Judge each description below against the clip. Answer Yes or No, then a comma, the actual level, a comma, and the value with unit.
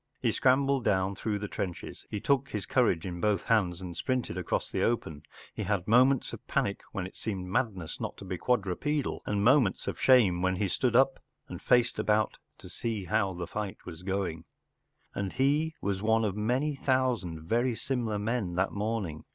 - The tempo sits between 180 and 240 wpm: Yes, average, 195 wpm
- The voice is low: Yes, low, 105 Hz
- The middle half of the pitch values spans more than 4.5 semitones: Yes, average, 5.0 semitones